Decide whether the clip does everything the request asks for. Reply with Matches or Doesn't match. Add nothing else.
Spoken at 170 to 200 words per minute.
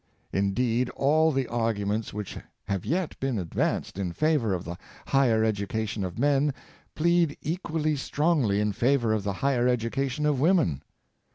Doesn't match